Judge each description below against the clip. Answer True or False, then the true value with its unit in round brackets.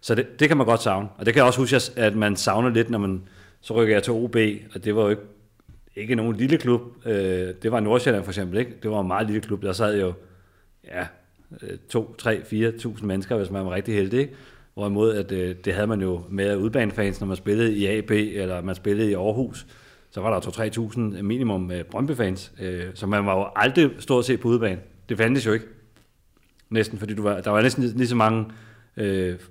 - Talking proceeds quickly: True (230 wpm)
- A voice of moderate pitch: False (105 Hz)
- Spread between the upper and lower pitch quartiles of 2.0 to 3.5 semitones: True (2.9 semitones)